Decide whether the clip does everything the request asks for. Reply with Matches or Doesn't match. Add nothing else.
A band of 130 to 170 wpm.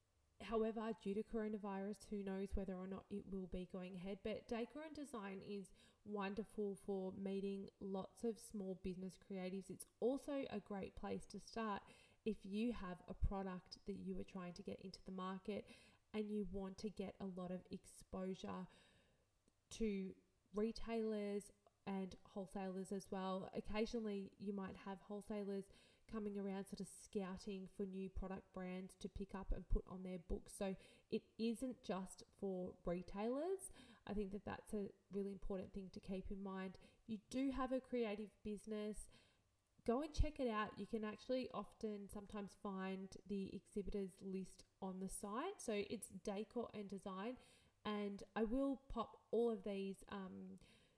Matches